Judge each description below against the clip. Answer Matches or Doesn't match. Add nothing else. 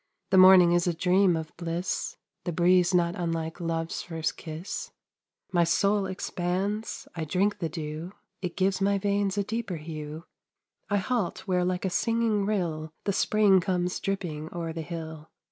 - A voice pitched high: Doesn't match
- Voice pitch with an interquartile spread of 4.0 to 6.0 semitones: Doesn't match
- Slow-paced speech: Doesn't match